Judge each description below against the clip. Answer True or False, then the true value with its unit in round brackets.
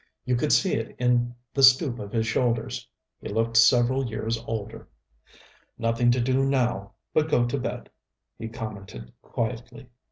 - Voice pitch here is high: False (120 Hz)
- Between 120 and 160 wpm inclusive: True (155 wpm)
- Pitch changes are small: True (2.1 semitones)